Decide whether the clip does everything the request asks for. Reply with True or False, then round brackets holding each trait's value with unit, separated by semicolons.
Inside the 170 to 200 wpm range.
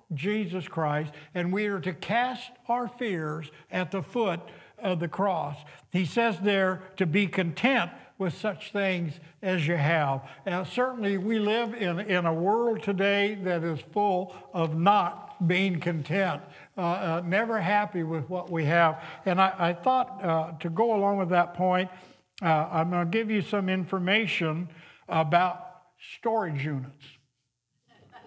False (155 wpm)